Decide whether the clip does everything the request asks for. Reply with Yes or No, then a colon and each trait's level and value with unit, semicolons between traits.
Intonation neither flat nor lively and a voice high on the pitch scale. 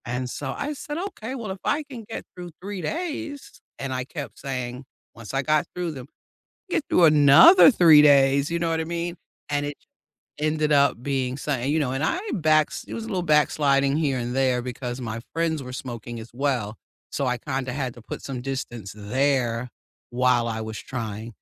No: average, 4.7 semitones; medium, 140 Hz